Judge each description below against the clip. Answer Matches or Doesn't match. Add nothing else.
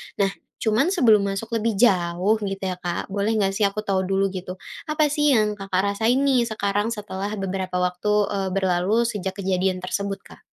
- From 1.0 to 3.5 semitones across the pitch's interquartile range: Matches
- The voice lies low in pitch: Doesn't match